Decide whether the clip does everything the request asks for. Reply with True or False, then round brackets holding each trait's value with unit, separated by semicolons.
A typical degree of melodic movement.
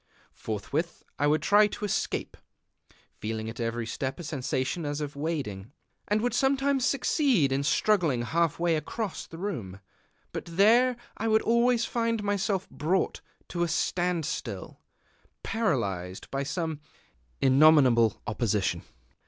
False (8.3 semitones)